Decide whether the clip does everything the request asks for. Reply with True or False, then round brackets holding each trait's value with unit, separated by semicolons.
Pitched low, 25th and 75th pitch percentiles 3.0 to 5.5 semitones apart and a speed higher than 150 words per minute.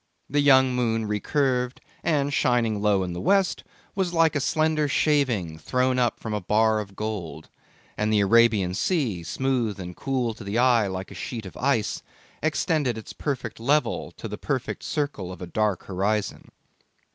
True (115 Hz; 5.1 semitones; 170 wpm)